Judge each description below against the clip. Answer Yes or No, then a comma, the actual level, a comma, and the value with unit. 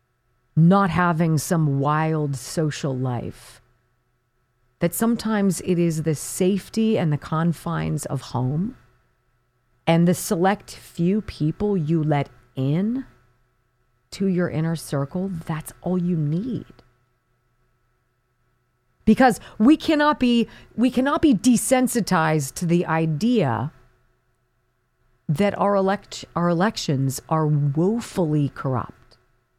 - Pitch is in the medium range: Yes, medium, 155 Hz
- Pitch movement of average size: No, wide, 7.6 semitones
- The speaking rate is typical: No, slow, 105 wpm